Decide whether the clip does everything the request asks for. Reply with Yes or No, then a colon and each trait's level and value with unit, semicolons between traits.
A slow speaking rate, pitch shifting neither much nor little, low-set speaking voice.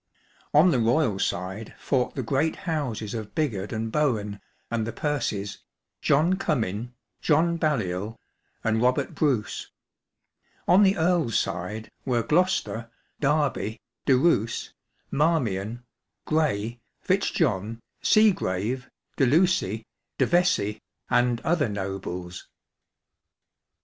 No: slow, 110 wpm; wide, 6.5 semitones; low, 125 Hz